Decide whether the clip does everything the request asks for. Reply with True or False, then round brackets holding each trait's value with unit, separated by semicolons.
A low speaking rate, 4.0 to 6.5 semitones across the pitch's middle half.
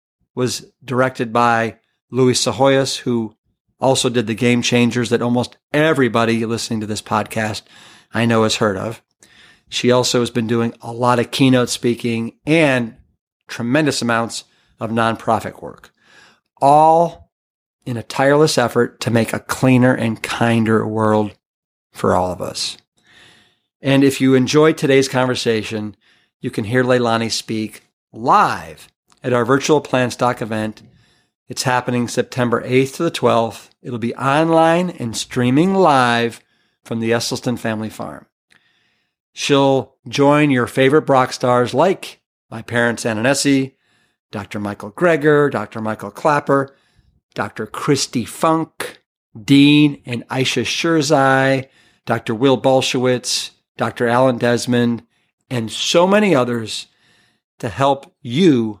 False (130 wpm; 2.8 semitones)